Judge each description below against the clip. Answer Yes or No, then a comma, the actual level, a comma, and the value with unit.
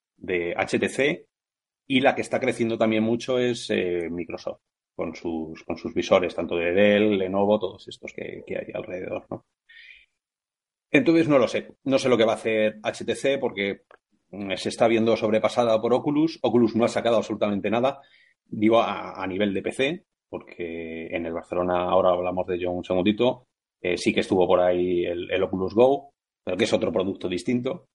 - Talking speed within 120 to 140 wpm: No, average, 180 wpm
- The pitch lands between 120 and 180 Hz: No, low, 105 Hz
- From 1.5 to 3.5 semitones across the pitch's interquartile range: No, average, 4.8 semitones